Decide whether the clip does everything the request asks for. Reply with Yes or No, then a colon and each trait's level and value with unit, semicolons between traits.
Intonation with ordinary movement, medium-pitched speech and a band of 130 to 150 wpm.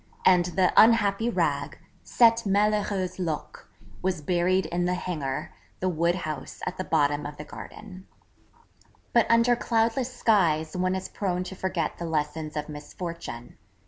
Yes: average, 4.1 semitones; medium, 180 Hz; average, 145 wpm